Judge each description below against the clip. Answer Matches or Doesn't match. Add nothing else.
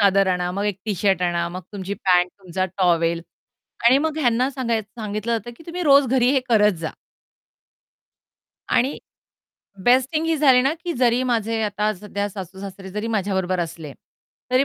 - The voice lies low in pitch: Doesn't match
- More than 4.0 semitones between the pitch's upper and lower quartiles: Matches